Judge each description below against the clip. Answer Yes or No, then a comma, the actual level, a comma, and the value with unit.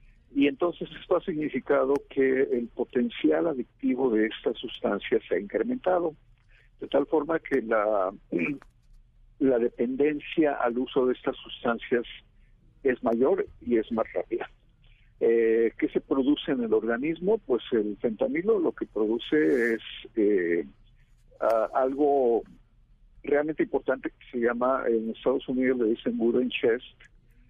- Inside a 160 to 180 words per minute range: No, average, 135 wpm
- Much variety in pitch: Yes, wide, 6.5 semitones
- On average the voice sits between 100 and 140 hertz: Yes, low, 135 Hz